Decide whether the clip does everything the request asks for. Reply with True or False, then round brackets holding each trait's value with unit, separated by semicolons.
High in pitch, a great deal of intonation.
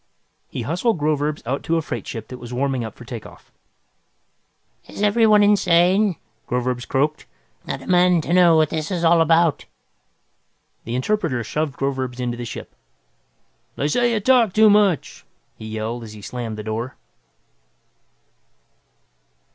False (150 Hz; 6.7 semitones)